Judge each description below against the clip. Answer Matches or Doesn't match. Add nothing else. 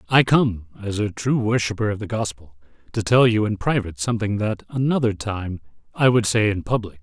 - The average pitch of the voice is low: Matches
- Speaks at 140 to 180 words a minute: Doesn't match